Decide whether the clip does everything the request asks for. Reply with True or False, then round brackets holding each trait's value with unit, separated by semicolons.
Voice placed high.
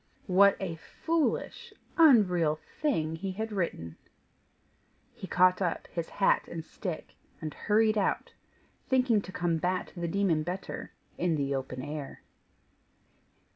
False (180 Hz)